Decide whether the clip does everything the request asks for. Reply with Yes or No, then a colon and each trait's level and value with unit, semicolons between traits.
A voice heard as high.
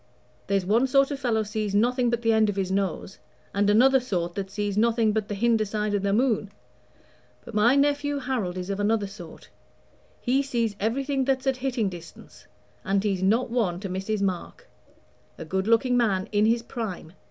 Yes: high, 215 Hz